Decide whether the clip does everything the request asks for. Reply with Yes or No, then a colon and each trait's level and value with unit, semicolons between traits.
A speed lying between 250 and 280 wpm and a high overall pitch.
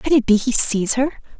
Yes: fast, 260 wpm; high, 245 Hz